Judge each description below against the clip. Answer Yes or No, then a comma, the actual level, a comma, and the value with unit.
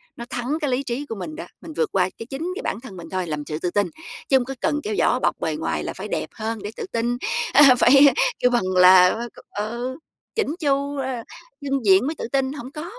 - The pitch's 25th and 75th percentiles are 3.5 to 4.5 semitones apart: No, average, 5.3 semitones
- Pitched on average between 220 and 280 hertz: Yes, very high, 250 Hz